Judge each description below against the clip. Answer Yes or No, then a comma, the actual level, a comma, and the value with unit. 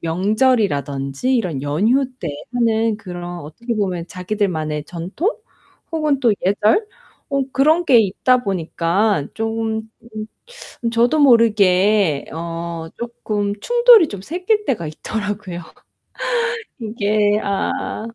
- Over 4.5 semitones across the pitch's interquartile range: Yes, average, 5.2 semitones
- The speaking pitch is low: No, high, 210 Hz